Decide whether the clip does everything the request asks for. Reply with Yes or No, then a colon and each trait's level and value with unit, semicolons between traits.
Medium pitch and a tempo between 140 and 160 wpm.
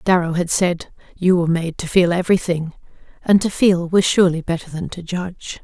No: medium, 175 Hz; average, 190 wpm